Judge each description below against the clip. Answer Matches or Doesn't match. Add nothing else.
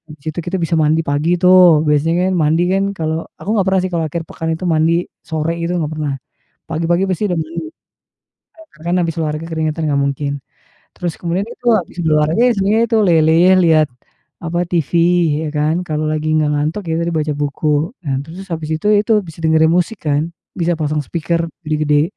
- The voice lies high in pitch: Doesn't match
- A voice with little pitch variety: Matches